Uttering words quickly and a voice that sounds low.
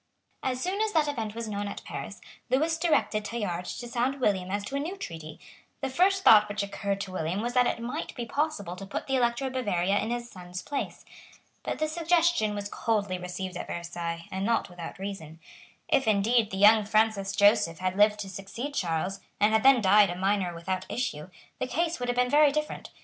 No: fast, 210 wpm; high, 210 Hz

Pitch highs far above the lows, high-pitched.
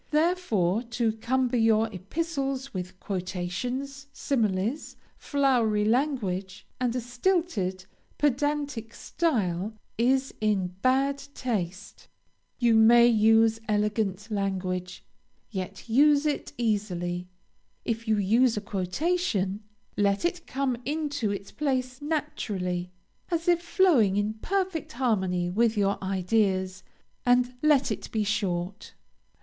Yes: wide, 5.8 semitones; high, 225 Hz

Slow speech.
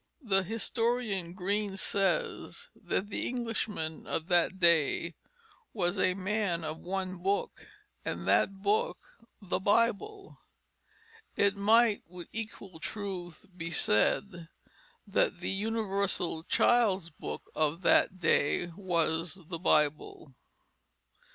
Yes: slow, 110 wpm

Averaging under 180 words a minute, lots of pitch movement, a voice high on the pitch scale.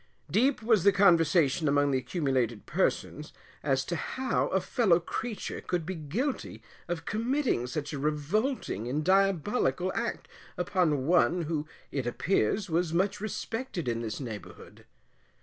No: average, 140 wpm; wide, 5.9 semitones; medium, 170 Hz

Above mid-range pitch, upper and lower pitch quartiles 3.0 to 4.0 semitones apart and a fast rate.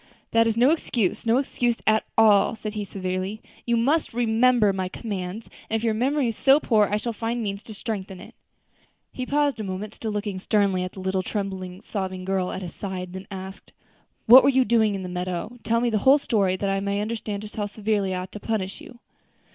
Yes: high, 210 Hz; average, 3.4 semitones; fast, 220 wpm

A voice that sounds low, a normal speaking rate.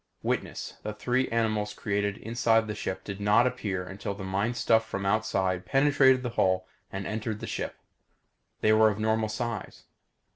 Yes: low, 110 Hz; average, 170 wpm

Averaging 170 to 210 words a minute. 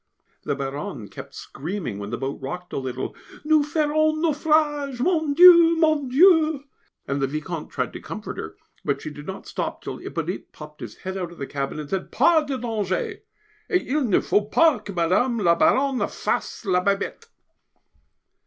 Yes: average, 180 wpm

